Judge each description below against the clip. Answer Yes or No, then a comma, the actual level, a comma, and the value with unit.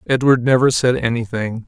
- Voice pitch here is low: Yes, low, 120 Hz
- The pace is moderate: Yes, average, 145 wpm